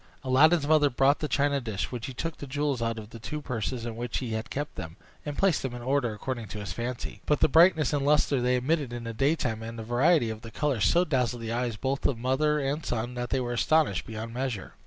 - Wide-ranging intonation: No, average, 4.0 semitones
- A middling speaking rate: No, fast, 250 wpm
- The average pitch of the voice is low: Yes, low, 125 Hz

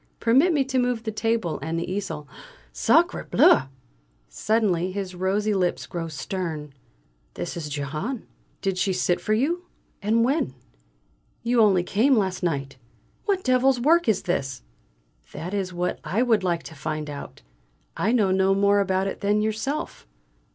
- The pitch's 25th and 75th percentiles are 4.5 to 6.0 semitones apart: Yes, average, 5.1 semitones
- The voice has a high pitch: Yes, high, 195 Hz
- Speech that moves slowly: No, average, 160 wpm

